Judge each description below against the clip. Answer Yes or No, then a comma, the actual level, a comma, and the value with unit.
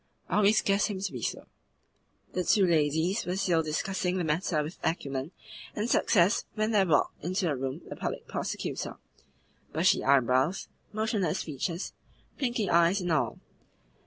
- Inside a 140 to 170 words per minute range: Yes, average, 155 wpm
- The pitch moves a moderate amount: Yes, average, 4.4 semitones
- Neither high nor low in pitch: Yes, medium, 180 Hz